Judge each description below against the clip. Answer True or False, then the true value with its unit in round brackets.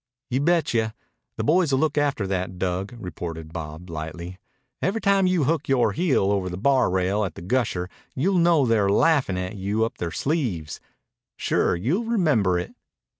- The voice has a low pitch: True (110 Hz)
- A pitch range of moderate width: False (8.8 semitones)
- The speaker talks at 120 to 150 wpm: False (165 wpm)